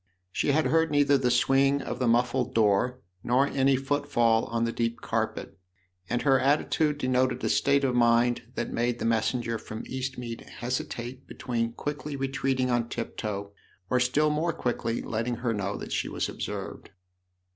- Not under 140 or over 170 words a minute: Yes, average, 165 wpm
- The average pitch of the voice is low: Yes, low, 125 Hz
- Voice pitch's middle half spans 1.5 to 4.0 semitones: Yes, narrow, 2.6 semitones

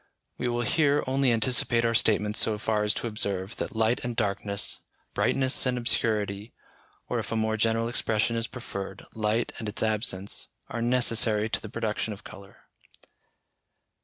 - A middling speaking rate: Yes, average, 160 wpm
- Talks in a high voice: No, low, 110 Hz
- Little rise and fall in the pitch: Yes, narrow, 2.1 semitones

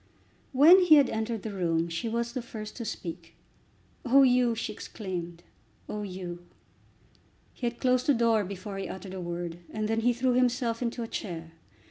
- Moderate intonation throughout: Yes, average, 4.9 semitones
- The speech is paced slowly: No, average, 180 wpm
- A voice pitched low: No, high, 220 Hz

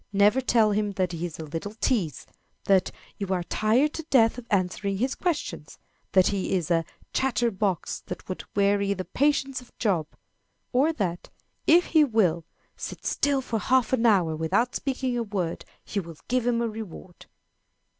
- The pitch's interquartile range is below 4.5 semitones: No, average, 5.2 semitones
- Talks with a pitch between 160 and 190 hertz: No, high, 210 Hz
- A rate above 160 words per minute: Yes, average, 175 wpm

